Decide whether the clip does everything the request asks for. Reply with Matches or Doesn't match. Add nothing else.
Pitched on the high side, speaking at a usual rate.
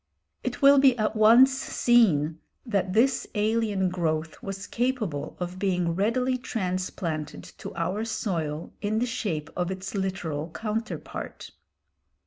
Doesn't match